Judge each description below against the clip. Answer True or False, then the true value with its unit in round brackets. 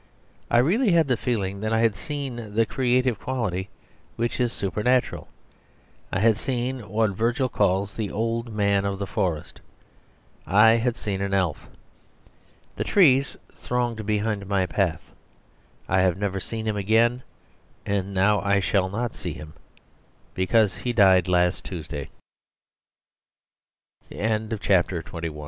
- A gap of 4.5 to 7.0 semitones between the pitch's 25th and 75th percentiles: False (3.6 semitones)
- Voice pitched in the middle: False (105 Hz)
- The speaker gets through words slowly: False (145 wpm)